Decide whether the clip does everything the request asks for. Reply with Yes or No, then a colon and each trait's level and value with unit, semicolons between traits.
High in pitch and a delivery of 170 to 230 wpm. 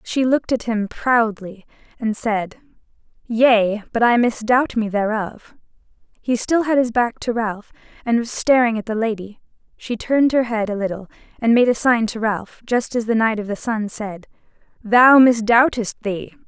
Yes: high, 230 Hz; average, 180 wpm